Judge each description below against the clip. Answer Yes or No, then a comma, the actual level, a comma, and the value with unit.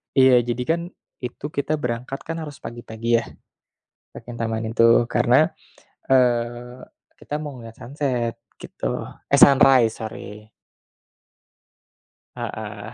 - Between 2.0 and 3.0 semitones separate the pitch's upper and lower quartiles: Yes, narrow, 2.6 semitones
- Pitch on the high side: No, low, 120 Hz